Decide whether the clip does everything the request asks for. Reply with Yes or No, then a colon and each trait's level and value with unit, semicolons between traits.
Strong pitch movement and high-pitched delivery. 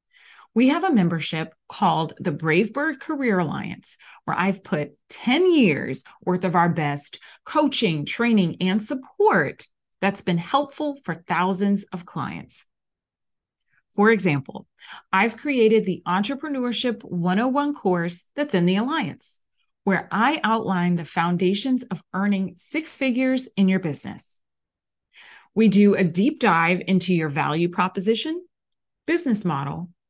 Yes: wide, 6.2 semitones; high, 195 Hz